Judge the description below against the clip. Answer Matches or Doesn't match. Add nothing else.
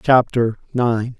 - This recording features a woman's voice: Doesn't match